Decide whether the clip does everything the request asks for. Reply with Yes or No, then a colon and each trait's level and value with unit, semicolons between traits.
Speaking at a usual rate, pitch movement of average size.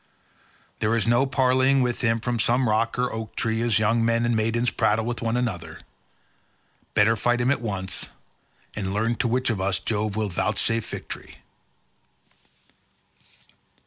No: average, 155 wpm; narrow, 2.1 semitones